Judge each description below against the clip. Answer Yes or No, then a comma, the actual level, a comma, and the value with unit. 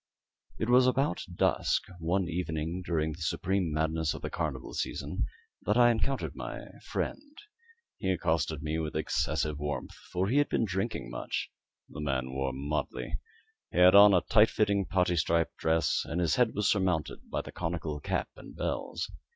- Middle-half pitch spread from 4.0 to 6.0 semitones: Yes, average, 4.5 semitones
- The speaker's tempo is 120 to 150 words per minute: No, average, 170 wpm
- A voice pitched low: Yes, very low, 85 Hz